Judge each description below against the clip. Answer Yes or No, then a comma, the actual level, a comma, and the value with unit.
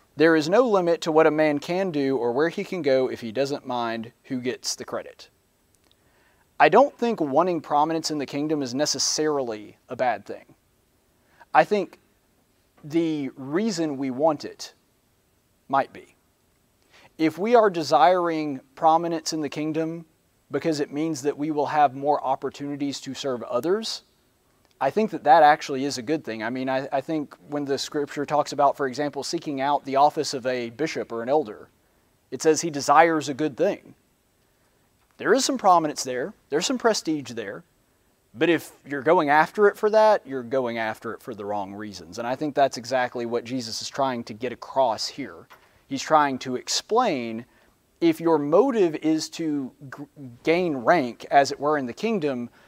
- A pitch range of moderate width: Yes, average, 3.5 semitones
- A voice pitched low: No, medium, 145 Hz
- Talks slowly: No, average, 180 wpm